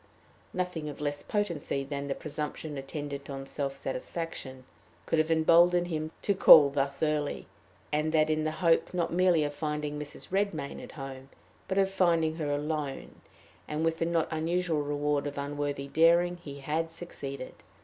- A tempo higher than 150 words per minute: Yes, average, 165 wpm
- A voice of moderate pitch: Yes, medium, 155 Hz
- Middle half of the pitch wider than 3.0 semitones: No, narrow, 2.5 semitones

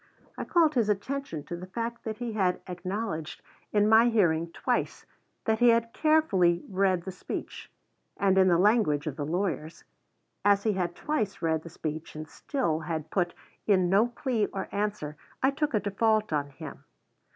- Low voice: No, high, 195 Hz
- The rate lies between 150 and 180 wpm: Yes, average, 175 wpm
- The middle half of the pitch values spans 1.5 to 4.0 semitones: No, average, 5.0 semitones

